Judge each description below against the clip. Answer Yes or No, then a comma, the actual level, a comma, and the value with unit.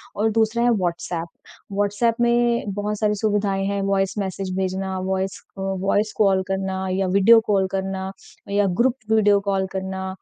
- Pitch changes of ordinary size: No, narrow, 1.7 semitones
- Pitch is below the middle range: No, high, 195 Hz